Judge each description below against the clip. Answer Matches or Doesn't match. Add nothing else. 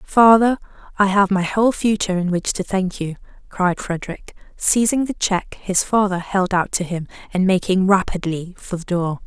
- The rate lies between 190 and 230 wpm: Doesn't match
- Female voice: Matches